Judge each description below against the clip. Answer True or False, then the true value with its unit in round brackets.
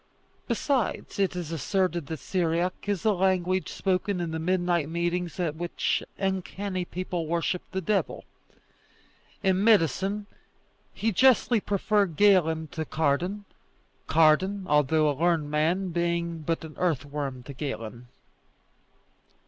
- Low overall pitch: False (175 Hz)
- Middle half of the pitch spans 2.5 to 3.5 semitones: True (3.2 semitones)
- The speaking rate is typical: False (125 wpm)